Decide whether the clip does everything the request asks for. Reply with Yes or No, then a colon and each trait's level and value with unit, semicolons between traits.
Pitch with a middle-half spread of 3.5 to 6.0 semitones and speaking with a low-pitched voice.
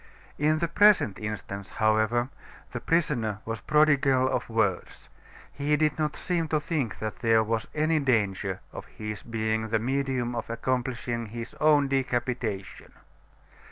Yes: average, 5.1 semitones; low, 120 Hz